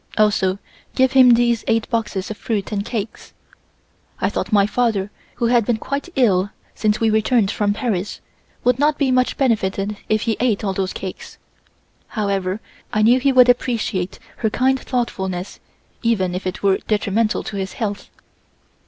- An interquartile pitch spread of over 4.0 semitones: No, average, 3.5 semitones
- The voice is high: Yes, high, 215 Hz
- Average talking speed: Yes, average, 165 wpm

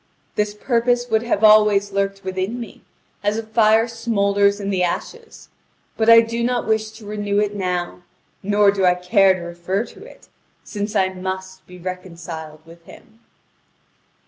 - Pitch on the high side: Yes, high, 200 Hz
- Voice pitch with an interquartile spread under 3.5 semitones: Yes, average, 2.8 semitones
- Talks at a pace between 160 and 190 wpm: Yes, average, 165 wpm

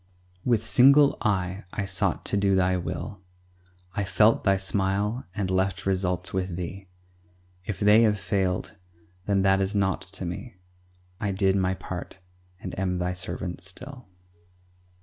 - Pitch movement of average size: No, narrow, 1.9 semitones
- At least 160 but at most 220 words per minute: No, average, 150 wpm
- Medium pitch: No, very low, 95 Hz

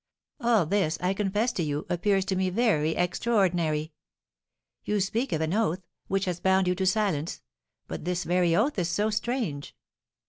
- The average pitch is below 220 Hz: Yes, medium, 185 Hz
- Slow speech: No, average, 170 wpm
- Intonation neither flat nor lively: Yes, average, 3.6 semitones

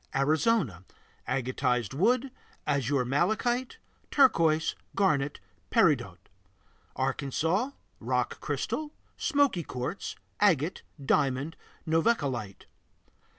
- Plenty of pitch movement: Yes, wide, 8.2 semitones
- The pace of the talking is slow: Yes, slow, 70 wpm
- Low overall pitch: No, medium, 155 Hz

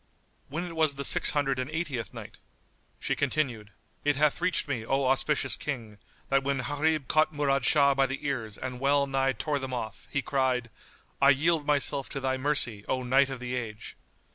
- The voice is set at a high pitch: No, low, 135 Hz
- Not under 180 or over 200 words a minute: Yes, average, 190 wpm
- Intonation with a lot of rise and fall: No, narrow, 2.4 semitones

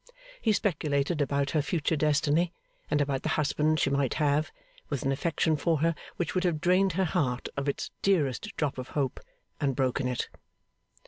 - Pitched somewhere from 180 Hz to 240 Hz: No, medium, 150 Hz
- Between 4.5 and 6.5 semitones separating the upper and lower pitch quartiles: No, average, 3.1 semitones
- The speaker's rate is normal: Yes, average, 180 wpm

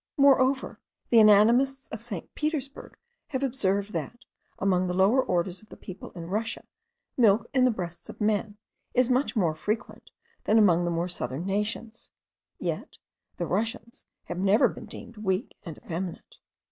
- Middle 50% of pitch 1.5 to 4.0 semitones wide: No, average, 4.8 semitones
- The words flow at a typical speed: Yes, average, 160 wpm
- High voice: Yes, high, 210 Hz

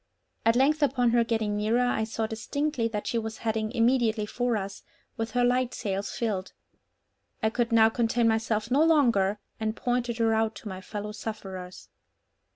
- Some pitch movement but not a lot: No, narrow, 2.1 semitones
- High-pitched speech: Yes, high, 225 Hz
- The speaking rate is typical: Yes, average, 170 wpm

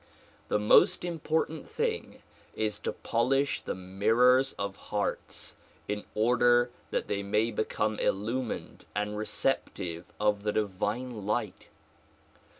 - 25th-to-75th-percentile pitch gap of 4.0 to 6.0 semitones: No, average, 3.3 semitones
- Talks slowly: Yes, slow, 115 wpm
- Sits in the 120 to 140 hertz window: No, low, 110 Hz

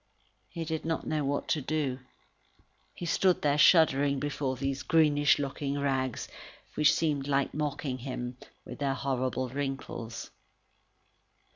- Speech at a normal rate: No, slow, 130 wpm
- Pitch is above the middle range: No, medium, 140 Hz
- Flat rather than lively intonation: Yes, narrow, 2.2 semitones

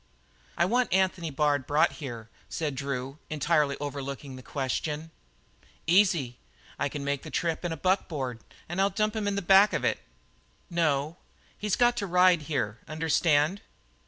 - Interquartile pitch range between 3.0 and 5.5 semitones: Yes, average, 4.8 semitones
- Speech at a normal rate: Yes, average, 160 wpm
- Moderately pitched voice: Yes, medium, 155 Hz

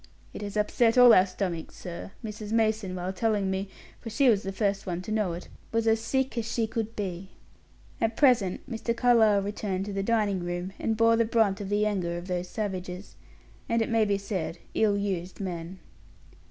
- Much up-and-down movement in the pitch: No, average, 3.1 semitones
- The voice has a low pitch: No, high, 205 Hz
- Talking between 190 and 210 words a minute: Yes, average, 200 wpm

